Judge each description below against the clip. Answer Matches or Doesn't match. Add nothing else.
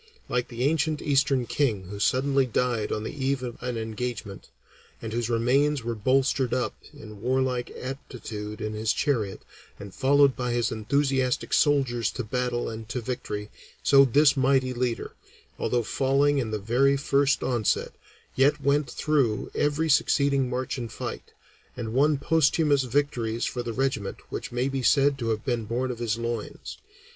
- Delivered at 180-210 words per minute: Doesn't match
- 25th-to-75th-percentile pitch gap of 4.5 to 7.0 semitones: Doesn't match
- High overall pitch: Doesn't match